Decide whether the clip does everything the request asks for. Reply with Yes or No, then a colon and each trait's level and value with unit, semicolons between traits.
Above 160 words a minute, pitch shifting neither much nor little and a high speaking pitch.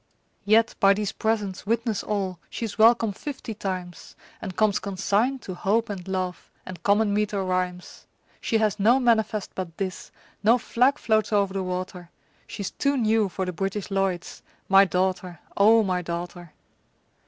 No: average, 155 wpm; average, 3.0 semitones; high, 200 Hz